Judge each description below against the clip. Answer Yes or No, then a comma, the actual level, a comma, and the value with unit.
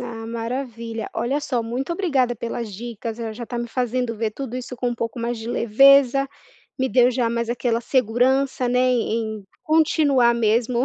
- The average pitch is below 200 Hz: No, high, 240 Hz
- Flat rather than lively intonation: Yes, narrow, 2.0 semitones